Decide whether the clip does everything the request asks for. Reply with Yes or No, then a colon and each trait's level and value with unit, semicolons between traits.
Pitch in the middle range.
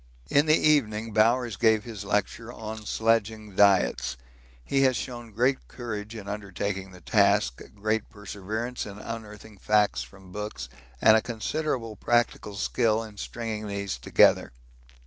No: low, 110 Hz